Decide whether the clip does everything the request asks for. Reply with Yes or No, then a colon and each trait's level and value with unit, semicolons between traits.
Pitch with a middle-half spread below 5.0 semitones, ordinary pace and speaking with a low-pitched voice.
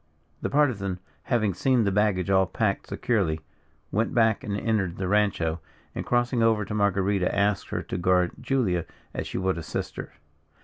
Yes: average, 3.3 semitones; average, 170 wpm; low, 100 Hz